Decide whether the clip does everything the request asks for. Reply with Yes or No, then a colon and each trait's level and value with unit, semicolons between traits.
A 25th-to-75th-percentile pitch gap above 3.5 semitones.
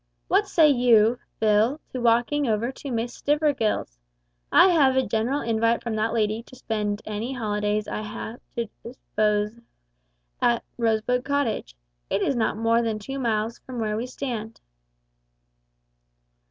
No: average, 2.9 semitones